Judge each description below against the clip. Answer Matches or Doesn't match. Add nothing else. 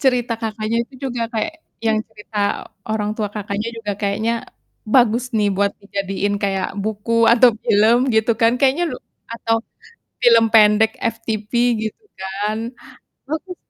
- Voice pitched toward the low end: Doesn't match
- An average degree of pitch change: Doesn't match